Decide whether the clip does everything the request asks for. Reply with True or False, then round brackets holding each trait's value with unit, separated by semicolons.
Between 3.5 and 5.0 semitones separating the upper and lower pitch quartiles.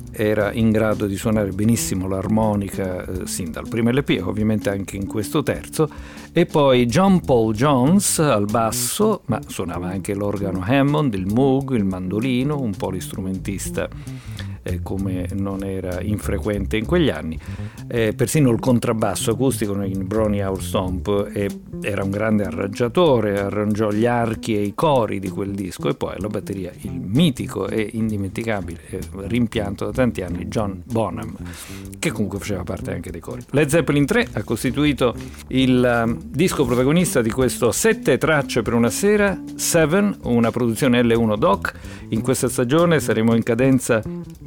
True (4.7 semitones)